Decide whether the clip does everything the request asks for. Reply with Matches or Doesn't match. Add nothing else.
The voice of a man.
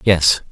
Matches